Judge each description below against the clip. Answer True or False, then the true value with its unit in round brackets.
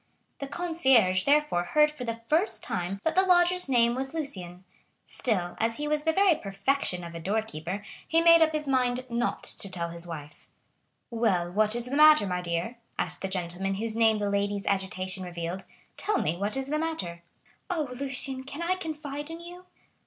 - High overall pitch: True (235 Hz)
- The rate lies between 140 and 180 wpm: False (190 wpm)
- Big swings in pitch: True (8.2 semitones)